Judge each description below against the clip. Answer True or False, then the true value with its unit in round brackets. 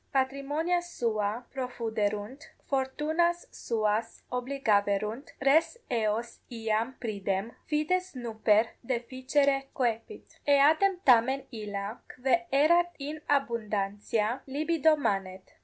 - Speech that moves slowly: True (90 wpm)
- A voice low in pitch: False (250 Hz)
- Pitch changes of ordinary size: True (4.8 semitones)